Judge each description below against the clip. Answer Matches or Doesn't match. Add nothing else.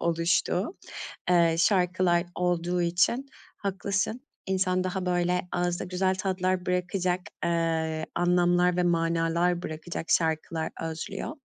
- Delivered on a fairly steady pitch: Matches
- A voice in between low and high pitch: Matches